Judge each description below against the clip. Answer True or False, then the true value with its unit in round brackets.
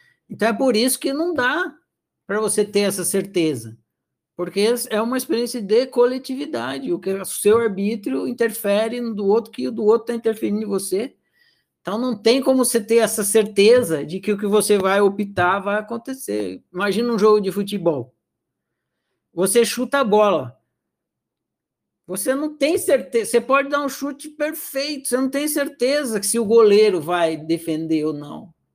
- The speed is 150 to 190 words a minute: True (175 wpm)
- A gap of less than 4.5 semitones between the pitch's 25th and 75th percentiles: False (4.8 semitones)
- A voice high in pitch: True (220 Hz)